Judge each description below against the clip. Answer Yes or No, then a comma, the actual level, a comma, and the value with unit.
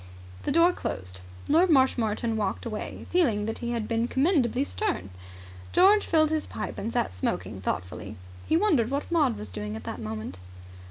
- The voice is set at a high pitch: Yes, high, 235 Hz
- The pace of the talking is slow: No, average, 170 wpm